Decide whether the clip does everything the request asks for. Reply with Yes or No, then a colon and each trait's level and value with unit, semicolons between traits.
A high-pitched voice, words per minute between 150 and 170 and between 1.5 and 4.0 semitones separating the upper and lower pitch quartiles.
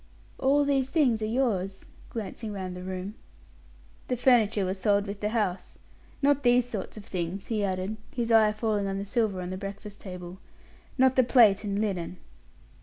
No: high, 210 Hz; average, 180 wpm; average, 3.7 semitones